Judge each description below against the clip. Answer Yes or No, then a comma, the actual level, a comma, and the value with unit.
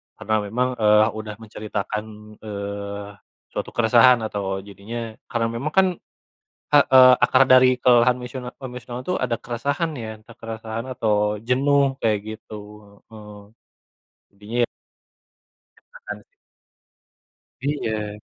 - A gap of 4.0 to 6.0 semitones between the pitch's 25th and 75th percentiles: No, average, 3.1 semitones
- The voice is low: Yes, low, 115 Hz